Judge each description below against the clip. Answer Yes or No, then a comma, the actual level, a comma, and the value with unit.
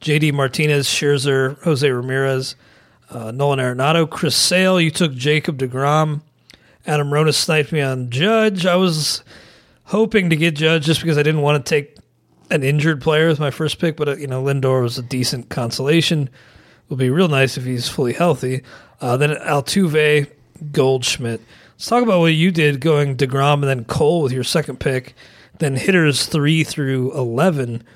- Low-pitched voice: No, medium, 145 Hz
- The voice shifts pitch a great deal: No, average, 3.3 semitones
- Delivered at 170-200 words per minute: Yes, average, 175 wpm